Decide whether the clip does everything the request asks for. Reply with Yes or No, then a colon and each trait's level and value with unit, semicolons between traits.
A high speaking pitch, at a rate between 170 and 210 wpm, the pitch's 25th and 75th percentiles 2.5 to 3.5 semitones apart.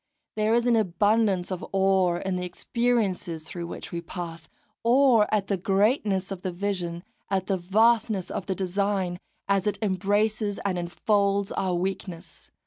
No: high, 195 Hz; average, 155 wpm; average, 2.9 semitones